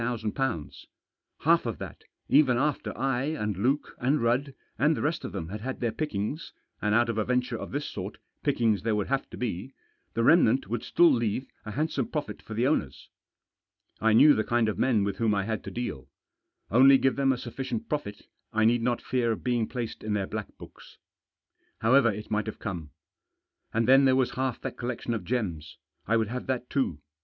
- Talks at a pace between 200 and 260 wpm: Yes, fast, 205 wpm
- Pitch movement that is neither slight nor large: Yes, average, 3.8 semitones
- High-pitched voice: No, low, 120 Hz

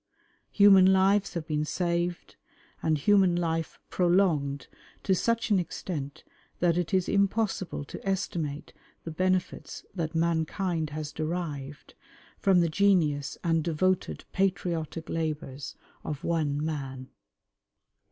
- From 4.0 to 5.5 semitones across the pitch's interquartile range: No, average, 3.5 semitones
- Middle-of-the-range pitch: Yes, medium, 170 Hz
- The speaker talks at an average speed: No, slow, 115 wpm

